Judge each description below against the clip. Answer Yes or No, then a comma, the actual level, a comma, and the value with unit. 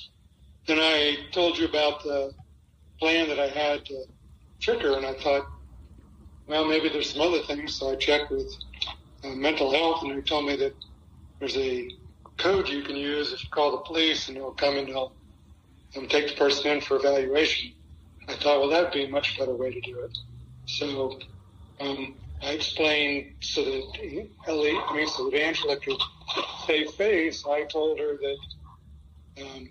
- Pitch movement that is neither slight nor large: No, wide, 8.5 semitones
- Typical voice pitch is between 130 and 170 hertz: Yes, medium, 140 Hz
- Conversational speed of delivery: Yes, average, 180 wpm